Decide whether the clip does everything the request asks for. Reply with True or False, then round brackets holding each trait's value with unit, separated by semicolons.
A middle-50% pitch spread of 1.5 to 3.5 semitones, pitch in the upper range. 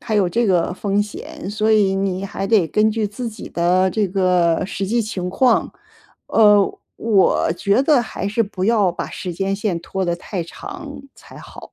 True (2.8 semitones; 200 Hz)